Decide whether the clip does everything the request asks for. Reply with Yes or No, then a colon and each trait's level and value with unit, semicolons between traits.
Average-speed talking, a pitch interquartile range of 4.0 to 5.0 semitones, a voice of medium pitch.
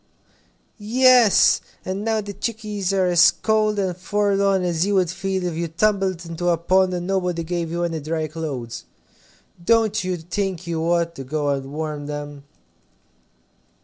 No: average, 160 wpm; average, 3.5 semitones; medium, 180 Hz